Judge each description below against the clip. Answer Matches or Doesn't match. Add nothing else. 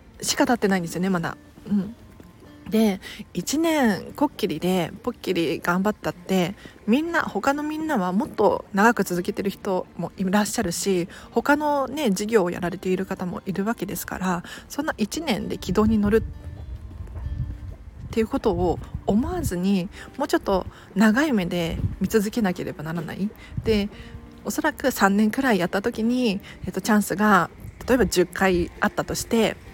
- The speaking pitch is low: Doesn't match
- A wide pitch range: Doesn't match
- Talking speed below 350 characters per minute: Matches